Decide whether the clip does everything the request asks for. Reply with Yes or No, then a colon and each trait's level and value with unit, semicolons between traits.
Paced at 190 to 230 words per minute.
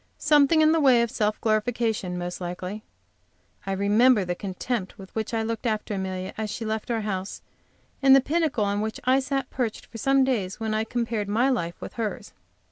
Yes: average, 200 wpm